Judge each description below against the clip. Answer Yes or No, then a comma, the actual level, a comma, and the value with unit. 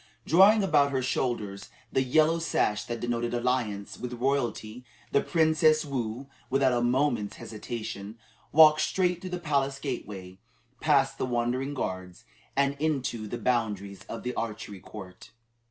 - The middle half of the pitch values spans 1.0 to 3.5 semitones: No, average, 4.7 semitones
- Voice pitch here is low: Yes, low, 125 Hz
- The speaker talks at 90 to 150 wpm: Yes, average, 140 wpm